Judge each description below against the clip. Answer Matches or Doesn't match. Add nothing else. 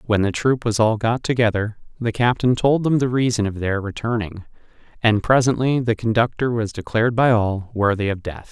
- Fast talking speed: Doesn't match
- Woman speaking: Doesn't match